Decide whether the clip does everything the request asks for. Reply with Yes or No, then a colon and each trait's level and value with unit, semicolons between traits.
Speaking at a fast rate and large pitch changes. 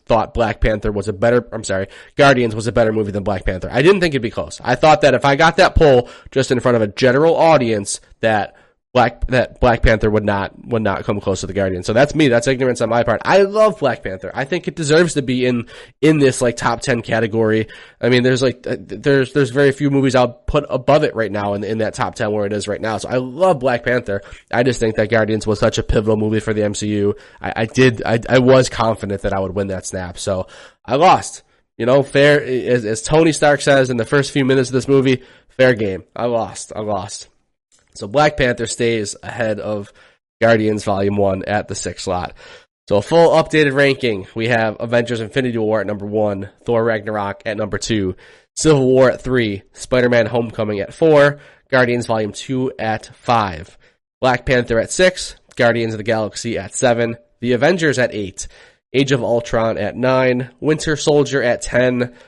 No: fast, 215 wpm; average, 3.8 semitones